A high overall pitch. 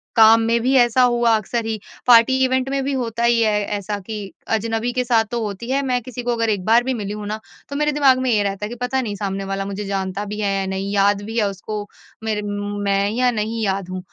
Yes: high, 225 Hz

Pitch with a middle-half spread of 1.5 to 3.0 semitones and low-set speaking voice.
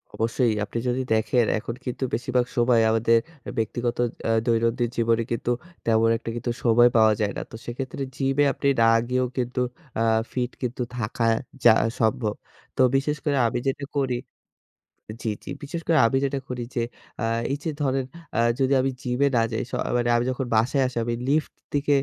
Yes: narrow, 2.5 semitones; low, 120 Hz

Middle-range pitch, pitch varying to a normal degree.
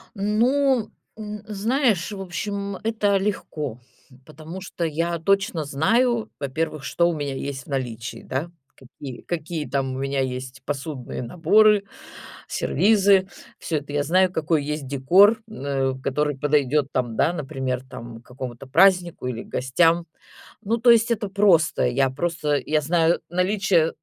No: medium, 160 Hz; wide, 6.4 semitones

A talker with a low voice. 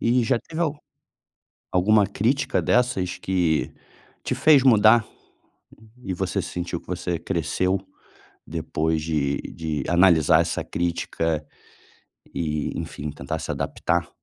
Yes: very low, 90 Hz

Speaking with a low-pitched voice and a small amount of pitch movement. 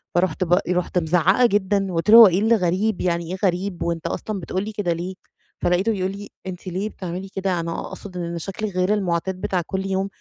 No: medium, 185 Hz; narrow, 2.2 semitones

